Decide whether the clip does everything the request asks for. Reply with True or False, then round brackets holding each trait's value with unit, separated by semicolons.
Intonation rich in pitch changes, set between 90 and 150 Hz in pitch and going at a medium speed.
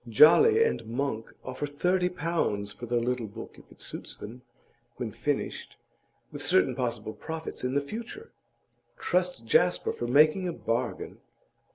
True (7.1 semitones; 135 Hz; 150 wpm)